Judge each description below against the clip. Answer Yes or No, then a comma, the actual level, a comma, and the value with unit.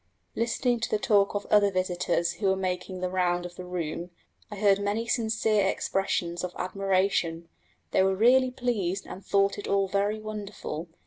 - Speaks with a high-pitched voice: Yes, high, 195 Hz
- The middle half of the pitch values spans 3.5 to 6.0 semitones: No, narrow, 2.6 semitones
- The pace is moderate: Yes, average, 175 wpm